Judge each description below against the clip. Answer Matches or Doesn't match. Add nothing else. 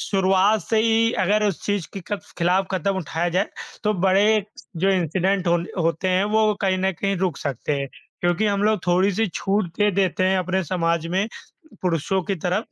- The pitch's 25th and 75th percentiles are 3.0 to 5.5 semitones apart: Doesn't match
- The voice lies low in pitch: Doesn't match